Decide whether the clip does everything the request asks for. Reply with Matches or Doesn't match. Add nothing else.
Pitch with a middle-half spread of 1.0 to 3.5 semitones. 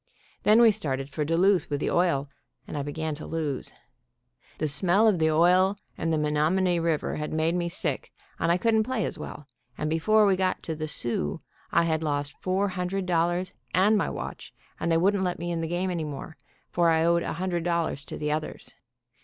Matches